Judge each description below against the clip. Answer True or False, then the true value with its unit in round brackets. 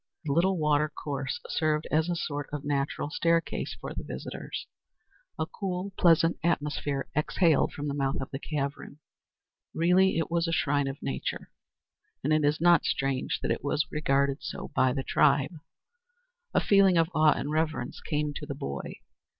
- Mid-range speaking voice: True (150 Hz)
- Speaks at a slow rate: False (165 wpm)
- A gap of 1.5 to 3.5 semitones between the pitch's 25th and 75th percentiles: True (2.9 semitones)